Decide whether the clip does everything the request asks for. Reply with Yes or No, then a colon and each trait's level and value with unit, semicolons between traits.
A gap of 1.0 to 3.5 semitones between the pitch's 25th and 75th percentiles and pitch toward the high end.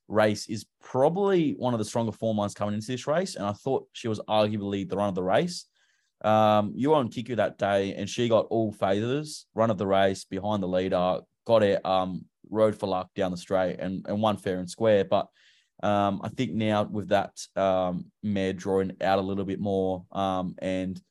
No: narrow, 2.5 semitones; low, 100 Hz